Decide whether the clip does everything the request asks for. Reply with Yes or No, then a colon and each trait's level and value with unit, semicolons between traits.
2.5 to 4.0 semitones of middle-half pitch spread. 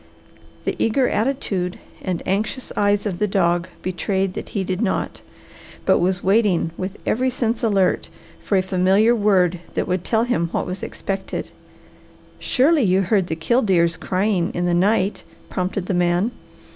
Yes: average, 3.1 semitones